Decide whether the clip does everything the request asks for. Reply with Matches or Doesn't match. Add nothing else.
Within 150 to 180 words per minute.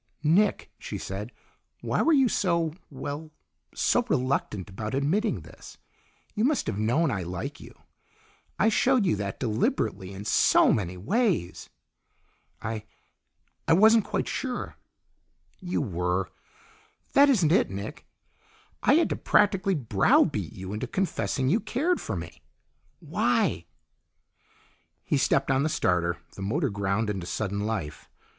Doesn't match